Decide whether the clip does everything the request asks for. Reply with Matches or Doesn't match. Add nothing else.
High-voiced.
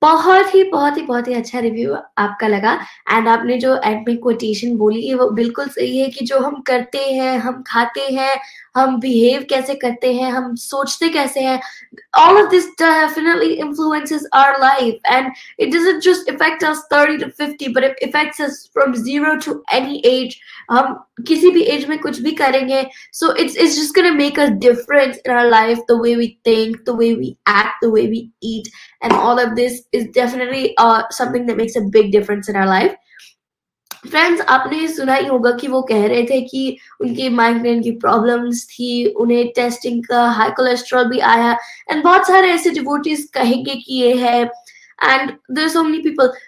Matches